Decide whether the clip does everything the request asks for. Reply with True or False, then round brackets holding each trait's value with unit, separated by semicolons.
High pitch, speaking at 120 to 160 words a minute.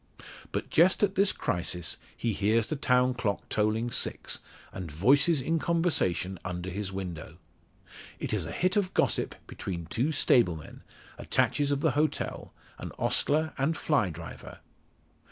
False (120 Hz; 150 wpm)